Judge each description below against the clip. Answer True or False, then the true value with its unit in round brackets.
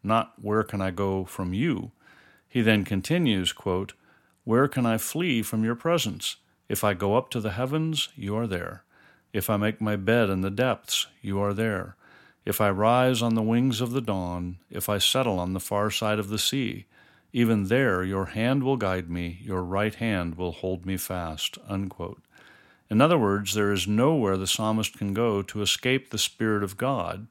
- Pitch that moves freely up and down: False (3.2 semitones)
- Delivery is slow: False (195 wpm)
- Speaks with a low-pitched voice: True (105 Hz)